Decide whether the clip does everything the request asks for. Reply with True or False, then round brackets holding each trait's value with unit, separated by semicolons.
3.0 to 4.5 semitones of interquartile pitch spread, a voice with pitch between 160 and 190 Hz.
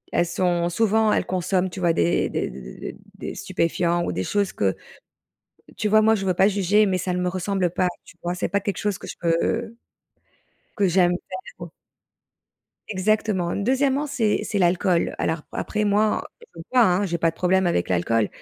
True (3.3 semitones; 185 Hz)